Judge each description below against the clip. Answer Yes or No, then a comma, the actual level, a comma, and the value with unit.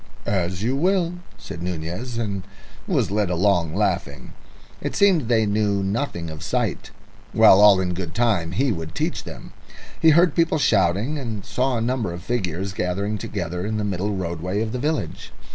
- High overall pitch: No, low, 100 Hz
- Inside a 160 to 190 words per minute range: Yes, average, 175 wpm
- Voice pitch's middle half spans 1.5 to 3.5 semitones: No, average, 5.2 semitones